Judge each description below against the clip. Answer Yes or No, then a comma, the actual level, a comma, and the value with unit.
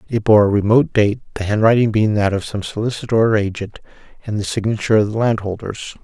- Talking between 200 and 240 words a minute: No, average, 190 wpm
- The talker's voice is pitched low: Yes, low, 105 Hz